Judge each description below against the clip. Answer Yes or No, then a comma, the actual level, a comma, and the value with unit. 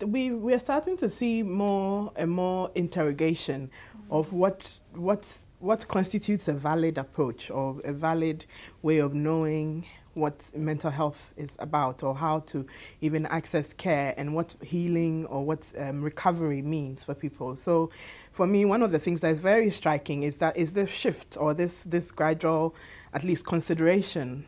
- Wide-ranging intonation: No, average, 3.7 semitones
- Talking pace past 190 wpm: No, average, 165 wpm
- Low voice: No, medium, 160 Hz